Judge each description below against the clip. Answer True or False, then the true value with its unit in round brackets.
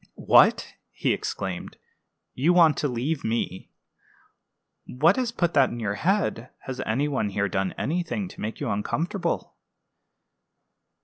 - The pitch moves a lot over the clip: True (7.8 semitones)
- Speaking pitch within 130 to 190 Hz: True (135 Hz)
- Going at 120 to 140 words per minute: True (135 wpm)